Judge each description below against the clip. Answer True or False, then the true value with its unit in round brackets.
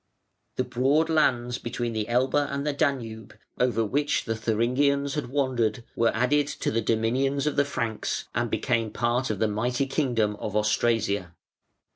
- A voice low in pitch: True (120 Hz)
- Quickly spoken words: False (160 wpm)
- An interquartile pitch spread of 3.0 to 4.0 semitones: True (3.7 semitones)